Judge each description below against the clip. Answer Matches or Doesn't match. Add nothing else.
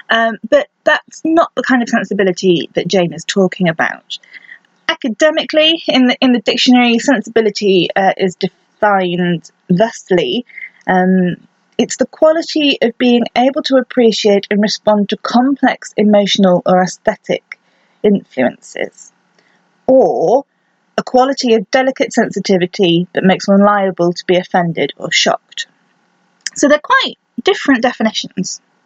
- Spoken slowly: Matches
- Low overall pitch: Doesn't match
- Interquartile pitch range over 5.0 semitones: Matches